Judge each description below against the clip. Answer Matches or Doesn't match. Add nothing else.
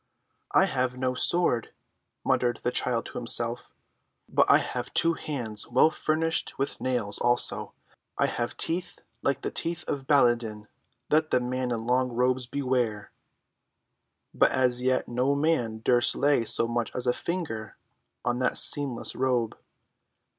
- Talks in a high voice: Doesn't match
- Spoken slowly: Doesn't match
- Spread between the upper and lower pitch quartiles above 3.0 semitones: Doesn't match